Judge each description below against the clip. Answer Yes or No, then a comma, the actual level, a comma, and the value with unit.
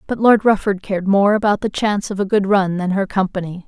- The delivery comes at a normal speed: No, fast, 245 wpm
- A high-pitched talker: Yes, high, 200 Hz